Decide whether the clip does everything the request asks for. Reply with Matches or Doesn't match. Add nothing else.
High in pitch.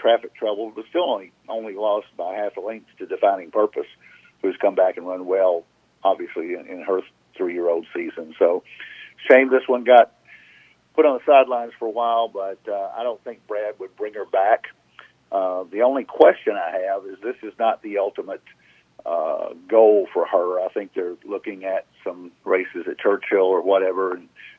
Matches